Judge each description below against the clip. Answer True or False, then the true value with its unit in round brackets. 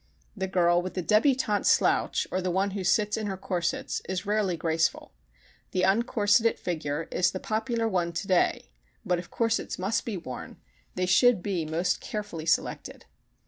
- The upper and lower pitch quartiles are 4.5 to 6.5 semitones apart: False (3.3 semitones)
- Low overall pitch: False (190 Hz)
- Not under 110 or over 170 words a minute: True (165 wpm)